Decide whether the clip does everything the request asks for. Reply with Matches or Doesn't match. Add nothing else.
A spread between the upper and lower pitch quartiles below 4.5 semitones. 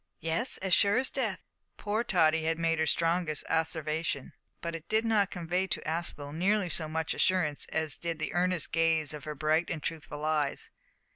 Matches